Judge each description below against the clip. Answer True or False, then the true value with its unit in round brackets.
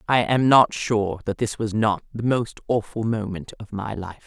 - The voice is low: True (110 Hz)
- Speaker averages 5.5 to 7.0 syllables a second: False (4.5 syllables/s)